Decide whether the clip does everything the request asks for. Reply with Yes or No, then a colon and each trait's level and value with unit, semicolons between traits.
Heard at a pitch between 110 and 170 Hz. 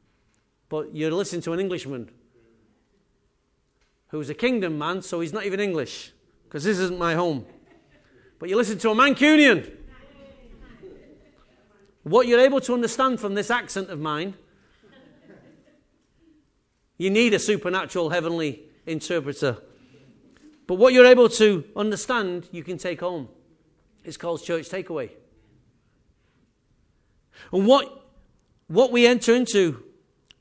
No: high, 190 Hz